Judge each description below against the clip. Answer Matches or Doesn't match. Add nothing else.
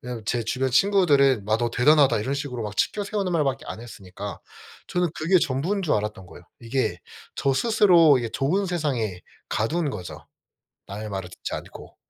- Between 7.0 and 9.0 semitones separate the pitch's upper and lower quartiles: Matches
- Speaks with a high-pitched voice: Doesn't match